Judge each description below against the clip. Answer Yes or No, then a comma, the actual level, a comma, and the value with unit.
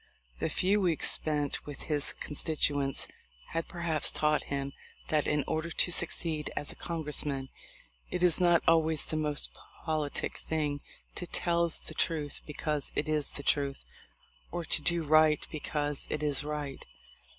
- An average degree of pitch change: No, narrow, 2.1 semitones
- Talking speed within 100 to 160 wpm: Yes, average, 155 wpm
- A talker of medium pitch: Yes, medium, 155 Hz